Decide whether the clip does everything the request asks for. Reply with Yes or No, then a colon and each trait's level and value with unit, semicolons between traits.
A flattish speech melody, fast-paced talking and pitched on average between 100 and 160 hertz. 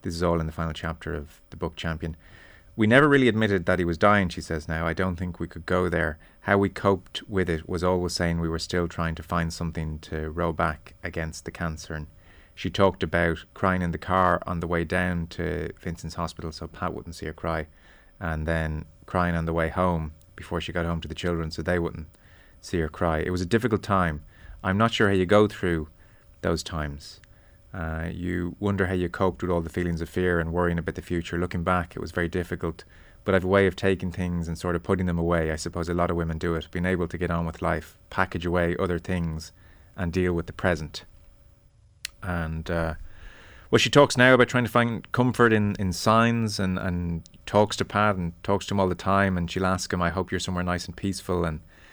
No: narrow, 2.3 semitones; fast, 235 wpm; very low, 90 Hz